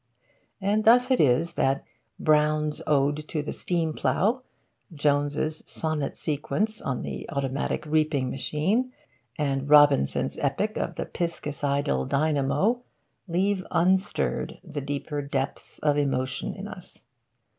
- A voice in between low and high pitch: Yes, medium, 150 Hz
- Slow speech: Yes, slow, 120 wpm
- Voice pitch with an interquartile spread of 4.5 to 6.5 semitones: No, average, 3.4 semitones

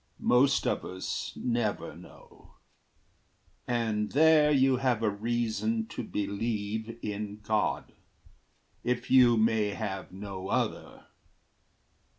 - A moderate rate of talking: No, slow, 105 wpm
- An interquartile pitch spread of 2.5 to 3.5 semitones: Yes, average, 2.8 semitones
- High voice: No, low, 110 Hz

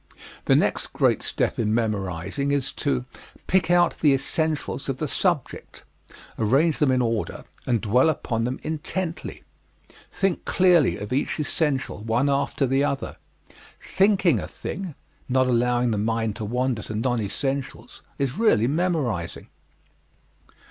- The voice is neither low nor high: No, low, 130 Hz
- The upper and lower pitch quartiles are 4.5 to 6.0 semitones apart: Yes, average, 5.2 semitones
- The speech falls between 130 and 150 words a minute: Yes, average, 140 wpm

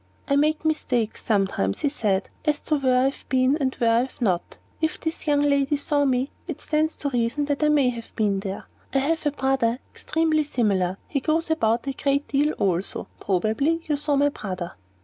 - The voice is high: Yes, very high, 275 Hz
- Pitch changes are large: No, average, 4.6 semitones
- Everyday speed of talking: No, fast, 210 wpm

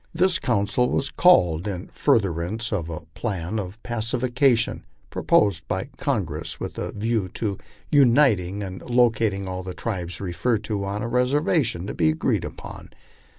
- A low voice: Yes, low, 105 Hz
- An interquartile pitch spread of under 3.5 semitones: No, average, 4.8 semitones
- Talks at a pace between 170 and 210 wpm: No, average, 150 wpm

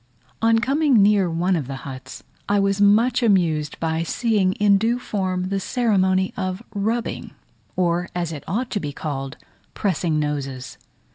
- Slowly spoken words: No, average, 155 wpm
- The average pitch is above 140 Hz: Yes, high, 190 Hz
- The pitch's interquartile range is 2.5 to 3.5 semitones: No, average, 4.7 semitones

